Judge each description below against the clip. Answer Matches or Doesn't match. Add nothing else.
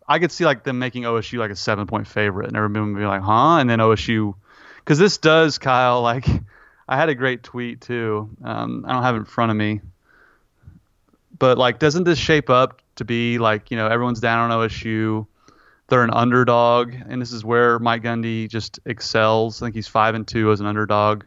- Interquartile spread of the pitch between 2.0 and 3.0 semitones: Matches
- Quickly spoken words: Matches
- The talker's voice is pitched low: Matches